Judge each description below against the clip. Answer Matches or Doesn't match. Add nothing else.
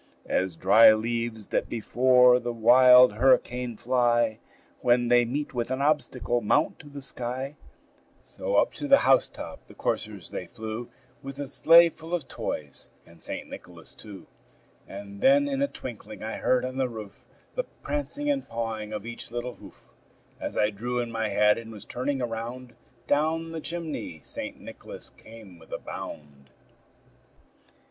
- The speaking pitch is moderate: Doesn't match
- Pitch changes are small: Doesn't match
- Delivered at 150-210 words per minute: Matches